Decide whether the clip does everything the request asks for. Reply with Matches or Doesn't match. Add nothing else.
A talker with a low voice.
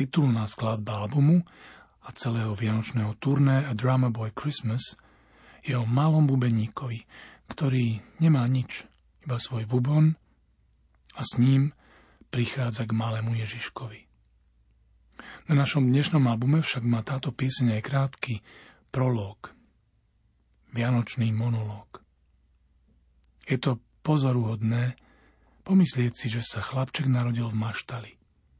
Matches